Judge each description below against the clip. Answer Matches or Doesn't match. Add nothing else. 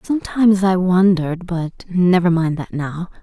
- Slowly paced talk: Matches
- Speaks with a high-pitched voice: Doesn't match